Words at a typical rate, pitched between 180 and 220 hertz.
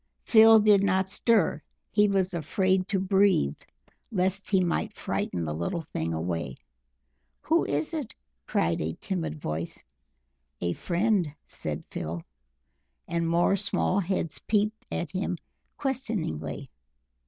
No: slow, 125 wpm; medium, 185 Hz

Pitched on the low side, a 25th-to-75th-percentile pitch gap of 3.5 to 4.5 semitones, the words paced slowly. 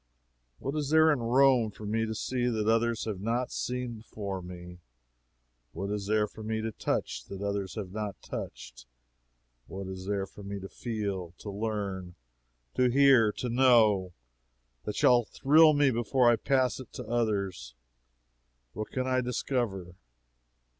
No: low, 110 Hz; average, 4.0 semitones; average, 155 wpm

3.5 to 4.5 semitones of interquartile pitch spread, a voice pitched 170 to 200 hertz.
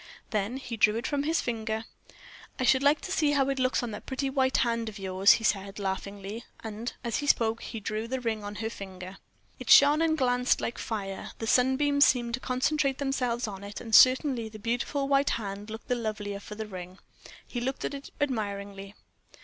No: average, 4.2 semitones; high, 230 Hz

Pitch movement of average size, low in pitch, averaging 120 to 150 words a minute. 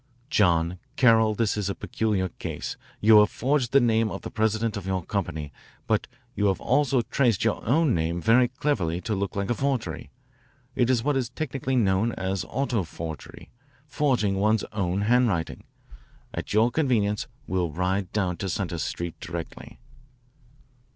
No: average, 4.7 semitones; low, 105 Hz; average, 160 wpm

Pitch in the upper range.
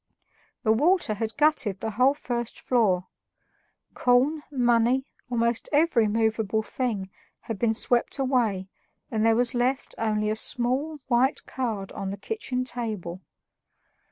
Yes: high, 235 Hz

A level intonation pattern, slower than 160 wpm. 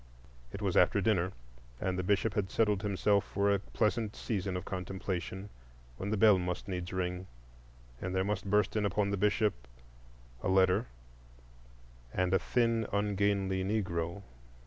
Yes: narrow, 1.9 semitones; average, 150 wpm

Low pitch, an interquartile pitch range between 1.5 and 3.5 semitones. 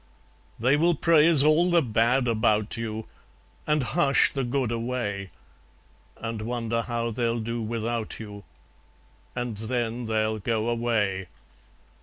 Yes: low, 115 Hz; narrow, 2.5 semitones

